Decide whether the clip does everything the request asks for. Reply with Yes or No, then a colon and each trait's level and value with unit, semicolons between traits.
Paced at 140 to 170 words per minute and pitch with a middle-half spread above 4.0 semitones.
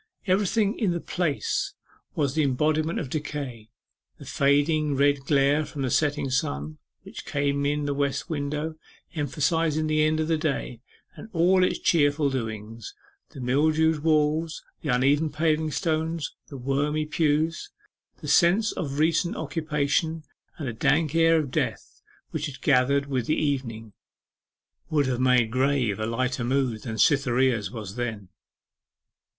No: average, 150 wpm; average, 3.2 semitones